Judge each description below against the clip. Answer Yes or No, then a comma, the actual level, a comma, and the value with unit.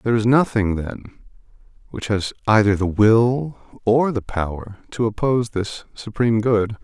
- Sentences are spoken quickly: No, average, 150 wpm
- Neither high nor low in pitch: No, low, 110 Hz